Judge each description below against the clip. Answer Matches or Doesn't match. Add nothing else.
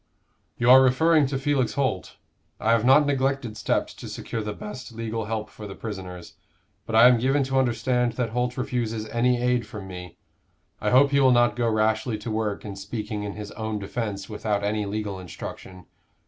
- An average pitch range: Matches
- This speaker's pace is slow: Doesn't match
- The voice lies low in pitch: Matches